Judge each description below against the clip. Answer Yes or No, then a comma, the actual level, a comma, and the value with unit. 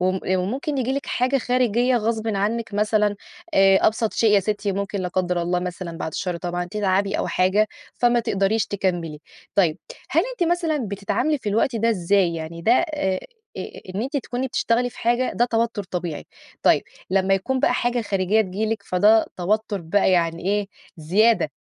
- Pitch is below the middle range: No, high, 205 Hz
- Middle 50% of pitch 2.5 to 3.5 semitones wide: No, average, 4.2 semitones